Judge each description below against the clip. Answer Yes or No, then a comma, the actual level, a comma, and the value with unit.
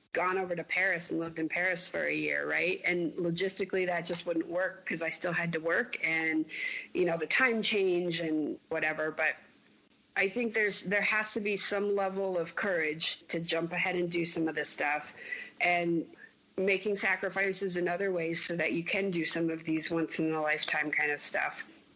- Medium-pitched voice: Yes, medium, 175 Hz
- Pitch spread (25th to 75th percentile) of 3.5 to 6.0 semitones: No, average, 3.0 semitones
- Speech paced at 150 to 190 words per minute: No, average, 200 wpm